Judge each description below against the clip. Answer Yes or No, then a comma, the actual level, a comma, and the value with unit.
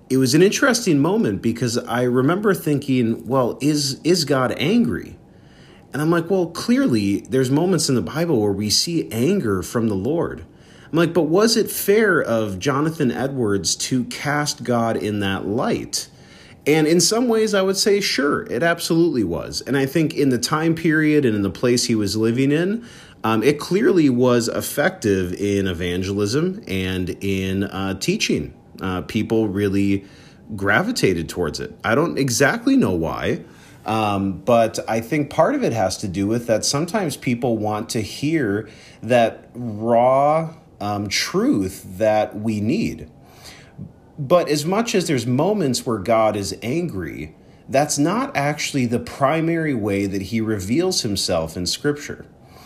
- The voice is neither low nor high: No, low, 125 Hz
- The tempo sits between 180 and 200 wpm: No, average, 160 wpm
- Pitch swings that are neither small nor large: No, wide, 7.0 semitones